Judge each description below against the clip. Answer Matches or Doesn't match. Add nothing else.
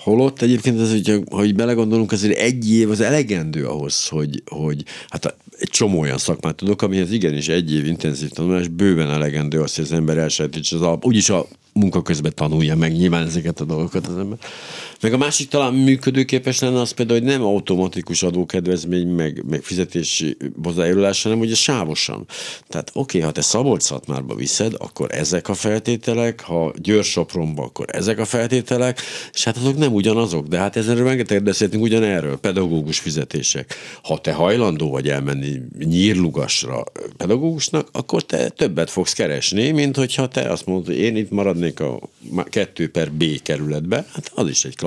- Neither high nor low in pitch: Doesn't match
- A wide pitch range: Matches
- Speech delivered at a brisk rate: Matches